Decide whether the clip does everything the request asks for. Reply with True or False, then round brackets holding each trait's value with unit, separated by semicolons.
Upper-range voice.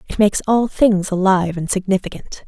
True (195 Hz)